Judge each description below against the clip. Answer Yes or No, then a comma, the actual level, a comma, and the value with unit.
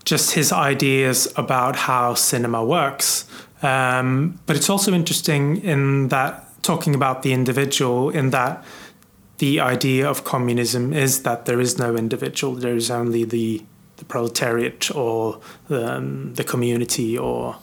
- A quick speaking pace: No, average, 145 wpm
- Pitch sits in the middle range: No, low, 130 Hz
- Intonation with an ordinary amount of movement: Yes, average, 3.0 semitones